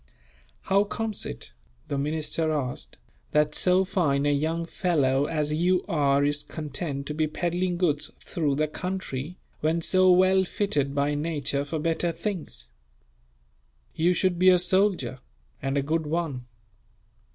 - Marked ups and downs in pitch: No, average, 4.0 semitones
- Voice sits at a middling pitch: Yes, medium, 155 Hz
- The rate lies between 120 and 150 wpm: Yes, average, 145 wpm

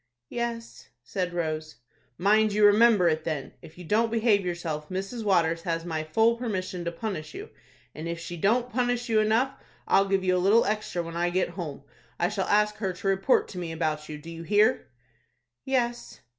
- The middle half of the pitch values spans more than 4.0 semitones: Yes, average, 4.6 semitones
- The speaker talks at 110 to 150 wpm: No, average, 195 wpm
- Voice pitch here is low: No, high, 190 Hz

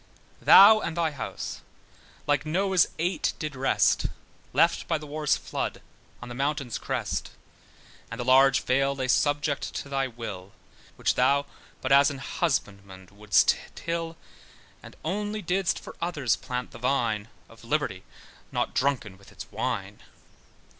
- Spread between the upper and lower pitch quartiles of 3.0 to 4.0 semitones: No, average, 4.7 semitones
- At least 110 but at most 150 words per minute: Yes, average, 145 wpm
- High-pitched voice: No, medium, 140 Hz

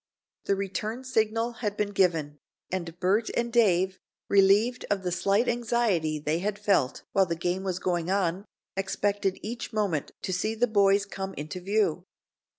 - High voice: Yes, high, 195 Hz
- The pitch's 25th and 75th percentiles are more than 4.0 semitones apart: No, average, 3.1 semitones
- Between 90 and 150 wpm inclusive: No, average, 160 wpm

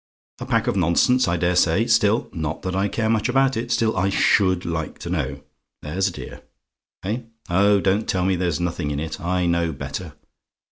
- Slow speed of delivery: No, average, 200 wpm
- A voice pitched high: No, very low, 95 Hz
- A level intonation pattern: No, average, 3.7 semitones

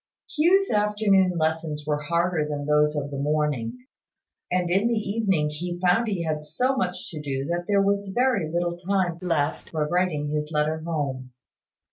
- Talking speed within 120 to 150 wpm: No, average, 170 wpm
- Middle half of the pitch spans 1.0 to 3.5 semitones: No, average, 4.4 semitones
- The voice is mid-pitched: Yes, medium, 170 Hz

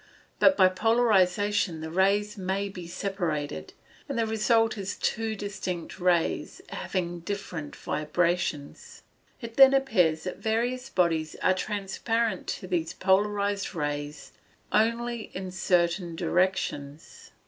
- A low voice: No, high, 190 Hz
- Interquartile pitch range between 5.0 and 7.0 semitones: No, average, 3.9 semitones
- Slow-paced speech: Yes, slow, 115 wpm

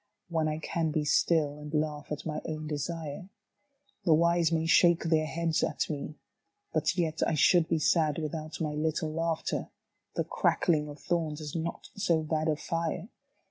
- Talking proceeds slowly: No, average, 175 wpm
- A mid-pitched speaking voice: Yes, medium, 160 Hz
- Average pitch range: No, narrow, 1.6 semitones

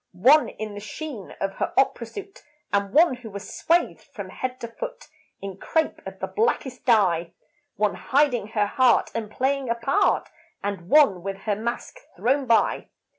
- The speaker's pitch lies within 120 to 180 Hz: No, high, 235 Hz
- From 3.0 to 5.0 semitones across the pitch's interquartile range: No, wide, 5.6 semitones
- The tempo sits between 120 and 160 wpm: No, average, 175 wpm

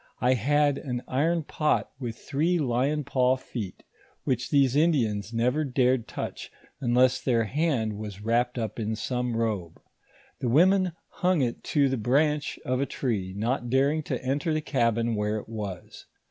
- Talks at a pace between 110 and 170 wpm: Yes, average, 160 wpm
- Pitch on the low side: Yes, low, 125 Hz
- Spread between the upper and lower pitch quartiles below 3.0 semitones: No, average, 4.0 semitones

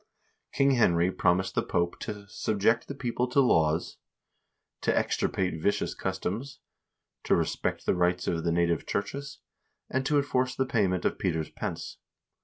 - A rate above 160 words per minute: No, average, 150 wpm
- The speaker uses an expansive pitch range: Yes, wide, 6.4 semitones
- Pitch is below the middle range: Yes, very low, 95 Hz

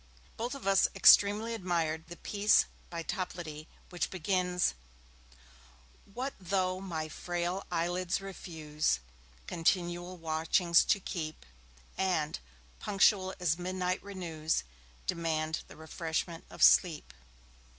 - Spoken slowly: Yes, slow, 105 wpm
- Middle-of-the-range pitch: Yes, medium, 175 Hz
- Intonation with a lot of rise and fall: No, average, 2.8 semitones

